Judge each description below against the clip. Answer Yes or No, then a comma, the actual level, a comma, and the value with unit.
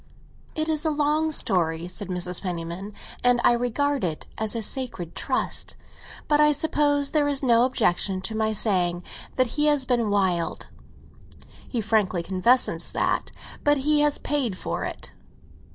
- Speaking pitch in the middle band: No, high, 235 Hz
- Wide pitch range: Yes, wide, 7.6 semitones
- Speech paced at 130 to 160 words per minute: Yes, average, 150 wpm